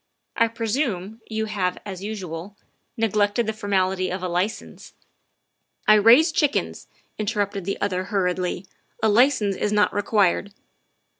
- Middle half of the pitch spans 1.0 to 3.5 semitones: Yes, narrow, 2.5 semitones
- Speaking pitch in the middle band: No, high, 205 Hz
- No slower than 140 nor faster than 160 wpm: Yes, average, 150 wpm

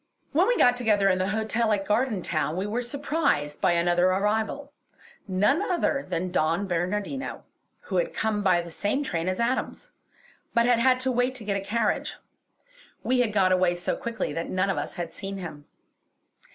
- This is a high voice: Yes, high, 205 Hz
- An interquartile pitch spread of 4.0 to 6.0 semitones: Yes, average, 5.2 semitones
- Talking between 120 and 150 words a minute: No, average, 185 wpm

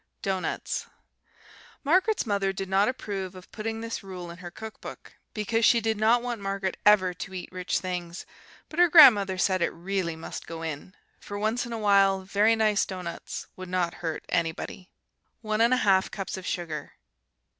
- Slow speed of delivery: No, average, 170 wpm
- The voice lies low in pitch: No, high, 195 Hz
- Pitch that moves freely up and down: No, average, 3.3 semitones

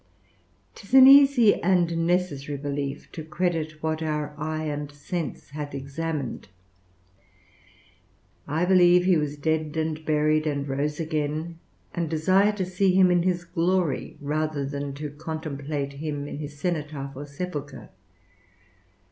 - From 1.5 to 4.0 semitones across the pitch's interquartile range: Yes, average, 3.2 semitones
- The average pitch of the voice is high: No, medium, 155 Hz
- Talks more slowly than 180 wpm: Yes, slow, 135 wpm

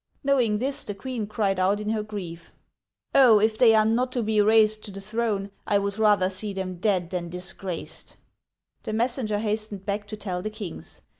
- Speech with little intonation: Yes, narrow, 2.2 semitones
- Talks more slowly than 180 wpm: No, average, 200 wpm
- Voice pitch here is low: No, high, 210 Hz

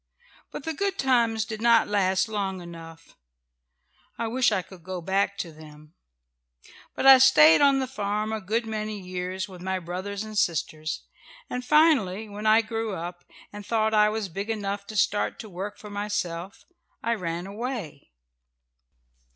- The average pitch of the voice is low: No, high, 205 Hz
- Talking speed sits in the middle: Yes, average, 165 wpm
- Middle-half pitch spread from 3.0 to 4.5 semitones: Yes, average, 3.4 semitones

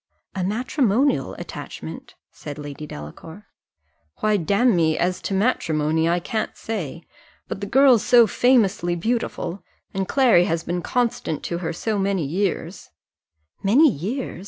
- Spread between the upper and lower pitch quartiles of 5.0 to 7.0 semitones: Yes, wide, 5.5 semitones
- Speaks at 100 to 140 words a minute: Yes, slow, 135 wpm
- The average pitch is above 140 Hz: Yes, high, 190 Hz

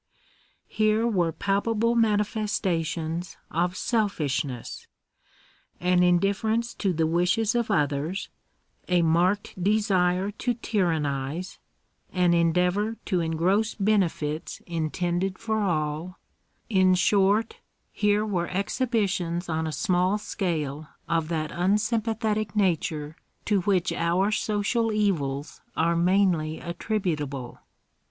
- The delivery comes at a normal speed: No, slow, 105 wpm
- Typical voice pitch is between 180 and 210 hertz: Yes, medium, 185 Hz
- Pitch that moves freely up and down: No, average, 4.1 semitones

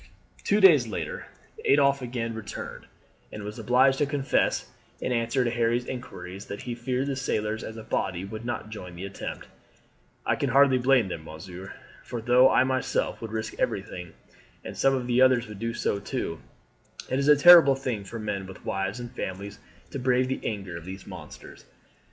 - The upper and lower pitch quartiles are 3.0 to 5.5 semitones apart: Yes, average, 4.4 semitones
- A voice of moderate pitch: No, low, 115 Hz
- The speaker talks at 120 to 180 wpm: No, average, 190 wpm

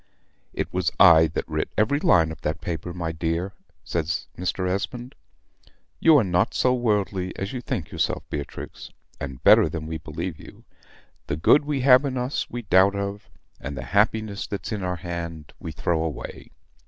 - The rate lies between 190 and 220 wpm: No, average, 180 wpm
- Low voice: Yes, very low, 90 Hz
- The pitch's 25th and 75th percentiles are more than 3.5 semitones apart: Yes, average, 4.8 semitones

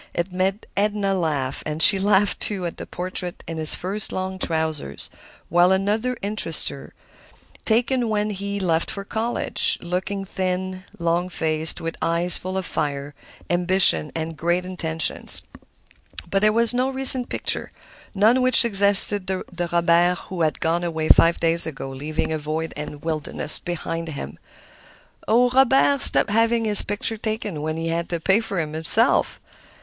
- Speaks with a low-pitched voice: No, medium, 180 Hz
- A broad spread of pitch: No, average, 4.2 semitones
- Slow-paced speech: No, average, 160 wpm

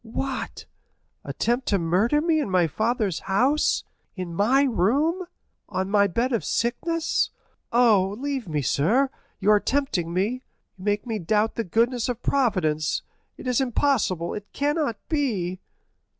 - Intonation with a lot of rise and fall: Yes, wide, 6.0 semitones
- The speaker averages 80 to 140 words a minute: Yes, slow, 135 wpm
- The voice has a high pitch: Yes, high, 225 Hz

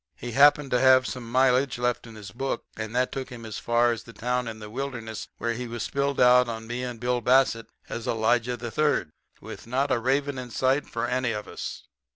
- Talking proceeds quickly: Yes, fast, 220 wpm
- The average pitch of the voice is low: Yes, low, 125 Hz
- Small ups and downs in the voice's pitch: Yes, narrow, 2.1 semitones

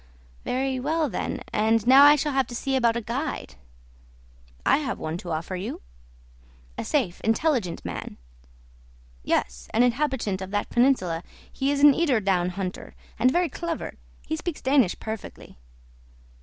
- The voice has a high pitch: Yes, high, 245 Hz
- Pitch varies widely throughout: Yes, wide, 6.5 semitones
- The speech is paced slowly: No, average, 155 wpm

